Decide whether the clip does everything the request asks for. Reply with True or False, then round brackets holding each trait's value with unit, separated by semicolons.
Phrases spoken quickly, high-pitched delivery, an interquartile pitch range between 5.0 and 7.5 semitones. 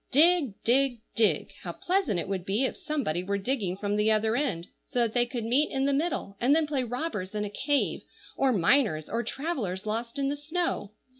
True (210 wpm; 240 Hz; 5.5 semitones)